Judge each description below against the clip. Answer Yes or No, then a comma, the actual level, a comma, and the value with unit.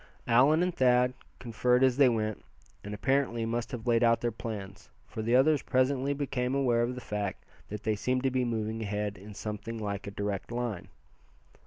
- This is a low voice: Yes, low, 120 Hz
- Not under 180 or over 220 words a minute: Yes, average, 190 wpm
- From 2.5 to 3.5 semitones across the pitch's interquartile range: Yes, average, 3.2 semitones